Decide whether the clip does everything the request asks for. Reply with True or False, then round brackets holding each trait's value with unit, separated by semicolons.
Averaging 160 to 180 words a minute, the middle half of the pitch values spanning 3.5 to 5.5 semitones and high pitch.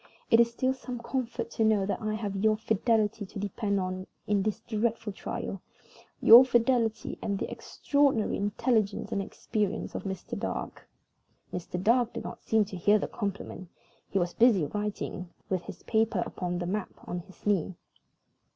False (170 wpm; 2.9 semitones; 210 Hz)